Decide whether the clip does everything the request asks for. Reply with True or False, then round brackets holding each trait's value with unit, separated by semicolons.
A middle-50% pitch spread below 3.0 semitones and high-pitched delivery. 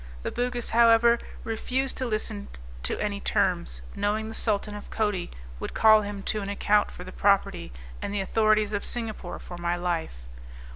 True (2.4 semitones; 210 Hz)